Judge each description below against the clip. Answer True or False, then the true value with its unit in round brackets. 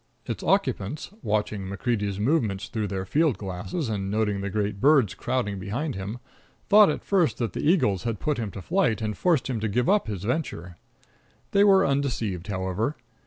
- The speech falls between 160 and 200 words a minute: True (180 wpm)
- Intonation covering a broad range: True (6.2 semitones)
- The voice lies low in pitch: True (110 Hz)